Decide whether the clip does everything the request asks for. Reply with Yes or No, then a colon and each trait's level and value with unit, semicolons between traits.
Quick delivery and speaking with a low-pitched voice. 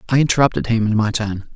Yes: fast, 230 wpm; low, 115 Hz